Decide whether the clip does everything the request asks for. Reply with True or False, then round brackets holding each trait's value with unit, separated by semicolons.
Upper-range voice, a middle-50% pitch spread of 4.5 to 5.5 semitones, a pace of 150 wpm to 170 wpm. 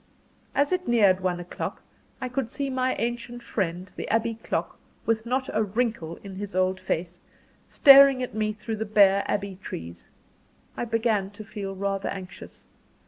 False (215 Hz; 4.0 semitones; 165 wpm)